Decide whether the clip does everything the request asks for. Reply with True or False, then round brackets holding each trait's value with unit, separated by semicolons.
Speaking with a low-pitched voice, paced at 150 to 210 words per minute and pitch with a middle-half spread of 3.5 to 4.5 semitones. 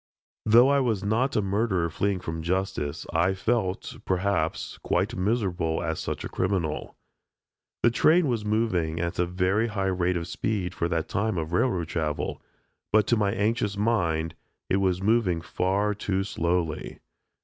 True (95 Hz; 160 wpm; 3.9 semitones)